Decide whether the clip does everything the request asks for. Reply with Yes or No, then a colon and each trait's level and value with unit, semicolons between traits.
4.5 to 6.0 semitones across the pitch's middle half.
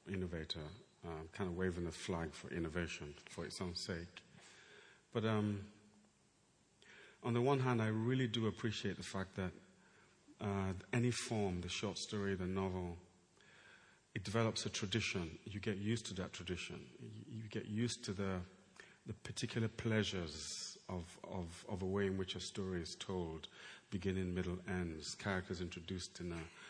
No: average, 3.4 semitones